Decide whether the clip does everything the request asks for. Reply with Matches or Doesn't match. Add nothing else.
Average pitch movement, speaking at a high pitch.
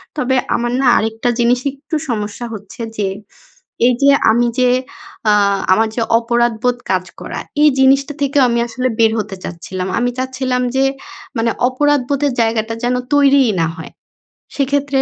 Matches